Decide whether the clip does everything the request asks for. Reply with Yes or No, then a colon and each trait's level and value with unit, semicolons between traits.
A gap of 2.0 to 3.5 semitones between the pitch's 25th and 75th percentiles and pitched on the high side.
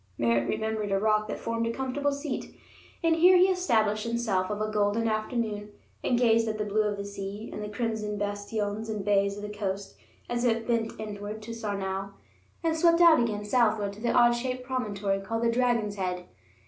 Yes: narrow, 2.6 semitones; high, 215 Hz